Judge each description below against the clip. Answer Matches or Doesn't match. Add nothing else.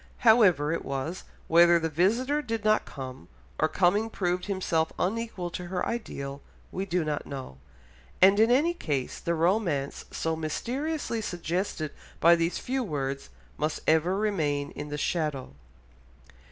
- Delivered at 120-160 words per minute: Matches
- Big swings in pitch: Matches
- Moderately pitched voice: Matches